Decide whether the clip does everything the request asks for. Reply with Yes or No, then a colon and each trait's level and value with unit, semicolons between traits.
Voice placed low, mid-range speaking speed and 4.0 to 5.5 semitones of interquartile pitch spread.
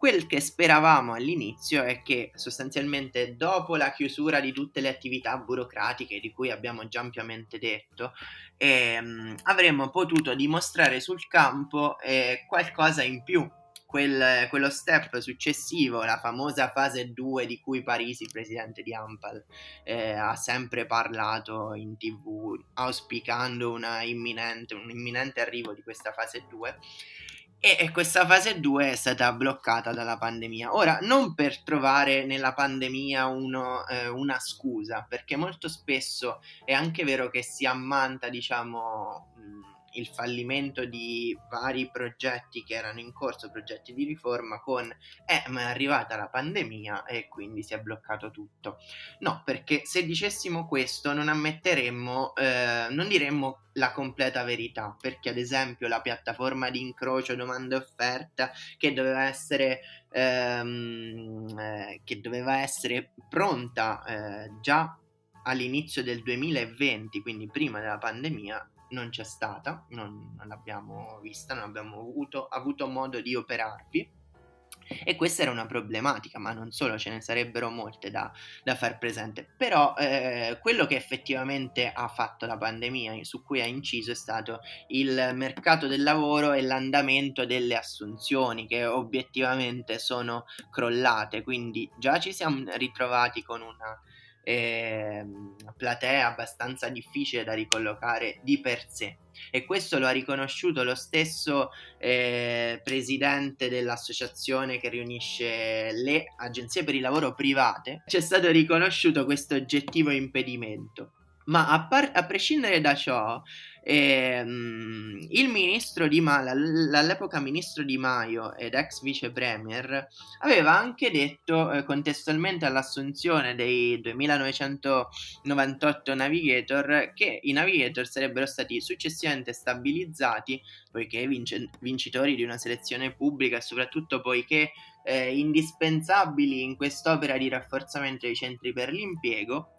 No: low, 130 Hz; average, 130 wpm; average, 3.4 semitones